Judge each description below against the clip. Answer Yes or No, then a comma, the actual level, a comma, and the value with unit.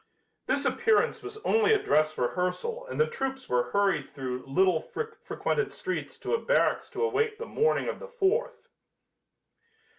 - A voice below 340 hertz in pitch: No, very high, 410 Hz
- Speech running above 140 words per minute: Yes, average, 155 wpm